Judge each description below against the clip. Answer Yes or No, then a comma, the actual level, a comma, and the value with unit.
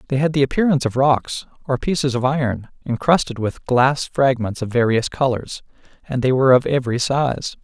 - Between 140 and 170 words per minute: No, average, 180 wpm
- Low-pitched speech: Yes, low, 130 Hz